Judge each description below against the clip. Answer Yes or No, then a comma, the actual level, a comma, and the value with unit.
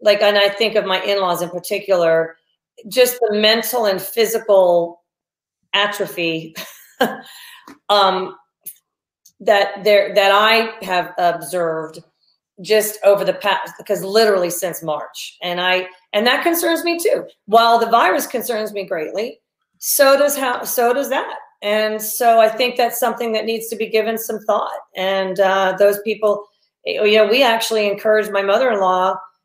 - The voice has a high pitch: Yes, high, 205 Hz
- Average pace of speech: Yes, average, 150 wpm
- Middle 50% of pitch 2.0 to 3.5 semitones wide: Yes, average, 3.1 semitones